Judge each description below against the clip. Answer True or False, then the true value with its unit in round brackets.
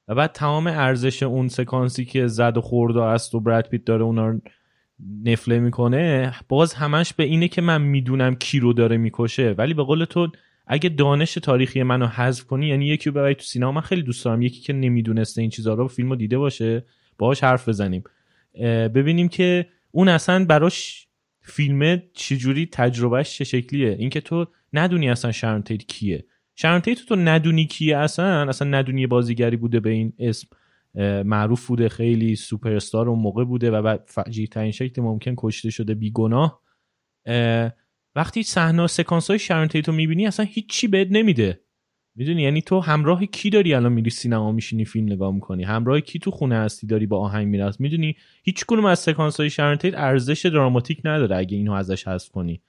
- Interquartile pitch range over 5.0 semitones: True (5.6 semitones)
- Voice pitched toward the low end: True (130 Hz)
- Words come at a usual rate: False (165 wpm)